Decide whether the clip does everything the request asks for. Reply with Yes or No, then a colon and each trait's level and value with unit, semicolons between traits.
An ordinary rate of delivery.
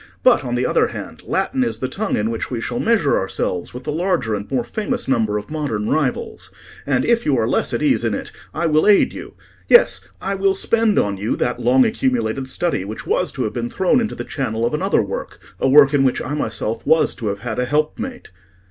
No: fast, 225 wpm